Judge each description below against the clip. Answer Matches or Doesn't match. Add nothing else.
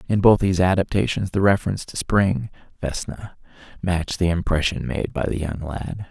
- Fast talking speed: Doesn't match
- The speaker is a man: Matches